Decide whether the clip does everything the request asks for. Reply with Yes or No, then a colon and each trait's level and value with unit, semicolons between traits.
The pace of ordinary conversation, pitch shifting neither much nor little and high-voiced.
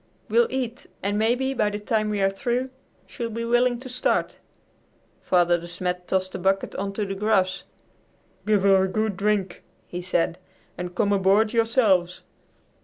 Yes: average, 170 wpm; average, 3.4 semitones; high, 205 Hz